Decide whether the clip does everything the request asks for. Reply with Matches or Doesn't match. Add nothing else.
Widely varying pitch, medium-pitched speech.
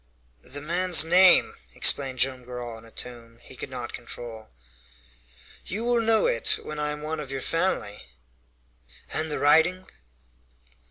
Matches